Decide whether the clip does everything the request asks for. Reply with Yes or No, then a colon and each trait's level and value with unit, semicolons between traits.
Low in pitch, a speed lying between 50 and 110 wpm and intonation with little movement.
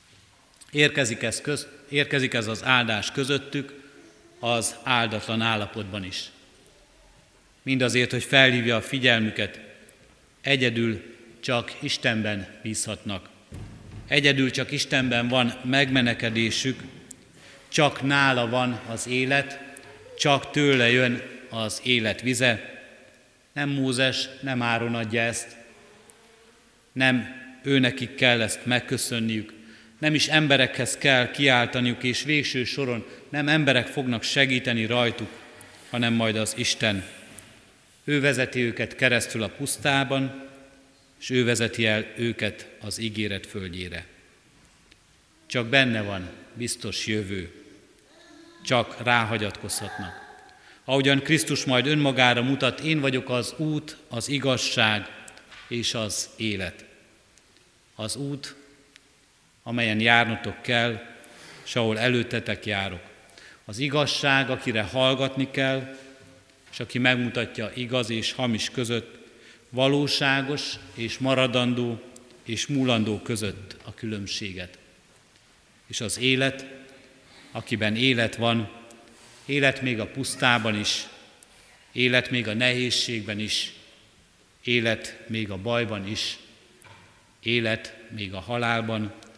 No: low, 120 Hz; slow, 105 wpm; average, 3.3 semitones